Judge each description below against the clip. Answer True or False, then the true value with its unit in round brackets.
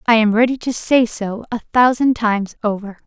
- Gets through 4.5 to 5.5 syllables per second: True (5.2 syllables/s)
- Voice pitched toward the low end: False (225 Hz)